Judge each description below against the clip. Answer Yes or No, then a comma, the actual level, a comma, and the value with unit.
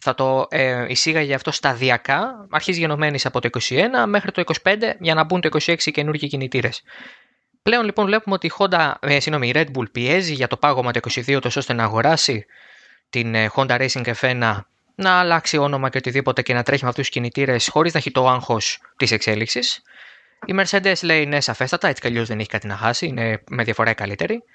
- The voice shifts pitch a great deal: No, average, 4.9 semitones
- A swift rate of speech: Yes, fast, 205 wpm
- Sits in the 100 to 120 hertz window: No, low, 135 Hz